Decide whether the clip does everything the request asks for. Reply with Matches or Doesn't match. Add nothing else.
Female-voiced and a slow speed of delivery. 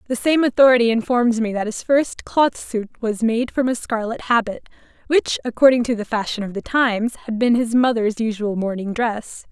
Doesn't match